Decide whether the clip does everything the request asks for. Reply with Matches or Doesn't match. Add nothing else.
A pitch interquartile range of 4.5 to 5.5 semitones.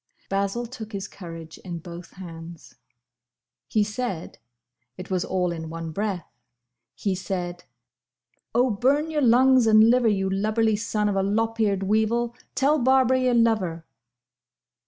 Matches